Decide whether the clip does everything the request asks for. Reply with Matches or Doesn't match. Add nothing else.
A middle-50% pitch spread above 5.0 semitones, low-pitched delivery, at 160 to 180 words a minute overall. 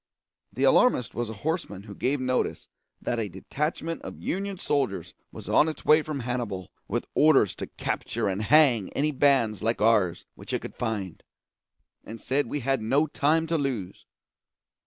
Matches